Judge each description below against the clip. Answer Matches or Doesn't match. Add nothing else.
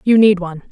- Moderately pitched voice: Doesn't match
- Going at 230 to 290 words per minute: Matches